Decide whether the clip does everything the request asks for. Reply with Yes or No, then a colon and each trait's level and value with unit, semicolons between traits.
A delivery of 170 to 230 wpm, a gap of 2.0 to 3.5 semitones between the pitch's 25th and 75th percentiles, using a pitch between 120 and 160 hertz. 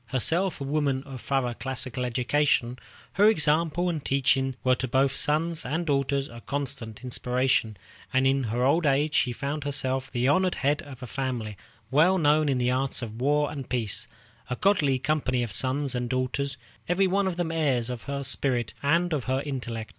Yes: average, 185 wpm; average, 2.8 semitones; low, 135 Hz